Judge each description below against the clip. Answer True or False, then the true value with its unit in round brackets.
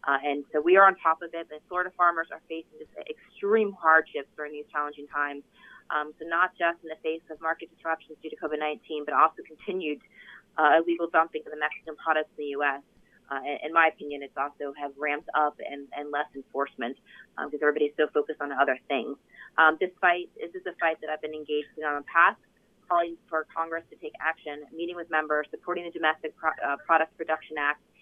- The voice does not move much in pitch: True (2.2 semitones)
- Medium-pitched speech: True (155 Hz)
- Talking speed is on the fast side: True (215 wpm)